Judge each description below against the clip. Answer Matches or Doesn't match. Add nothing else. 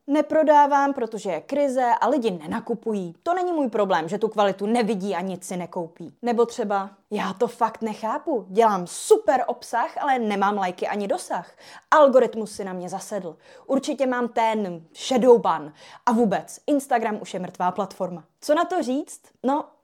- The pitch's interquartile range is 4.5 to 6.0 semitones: Matches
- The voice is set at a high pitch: Matches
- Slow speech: Doesn't match